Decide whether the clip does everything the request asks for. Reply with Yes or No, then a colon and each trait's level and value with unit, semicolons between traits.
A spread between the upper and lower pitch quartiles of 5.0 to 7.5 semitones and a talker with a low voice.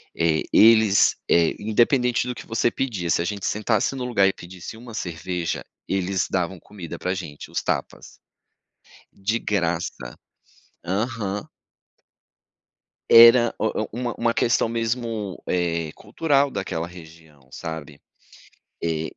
Yes: wide, 5.4 semitones; low, 100 Hz